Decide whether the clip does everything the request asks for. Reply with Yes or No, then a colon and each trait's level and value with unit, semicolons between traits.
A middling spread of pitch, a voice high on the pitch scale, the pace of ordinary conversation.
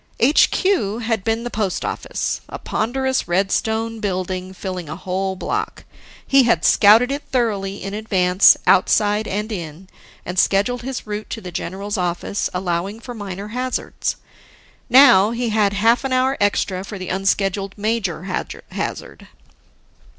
Yes: average, 3.4 semitones; high, 205 Hz; average, 145 wpm